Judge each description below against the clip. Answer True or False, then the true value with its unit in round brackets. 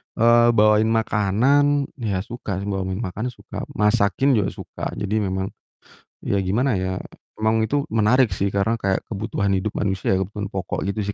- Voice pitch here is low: True (105 Hz)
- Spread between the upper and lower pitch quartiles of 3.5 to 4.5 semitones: False (2.8 semitones)